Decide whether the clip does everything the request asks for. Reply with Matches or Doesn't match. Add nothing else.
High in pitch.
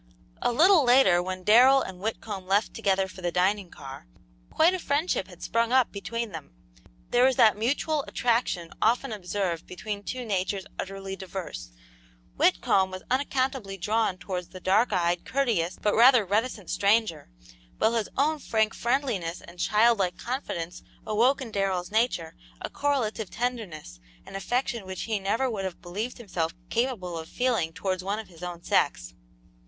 Matches